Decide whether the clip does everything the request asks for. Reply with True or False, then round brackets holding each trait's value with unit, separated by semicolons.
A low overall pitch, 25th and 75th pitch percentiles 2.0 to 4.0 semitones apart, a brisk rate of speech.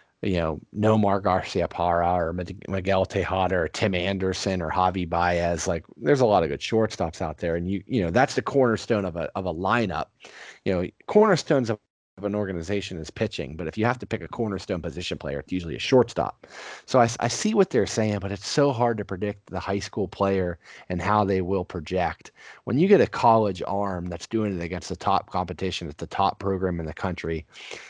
True (95 Hz; 2.9 semitones; 215 wpm)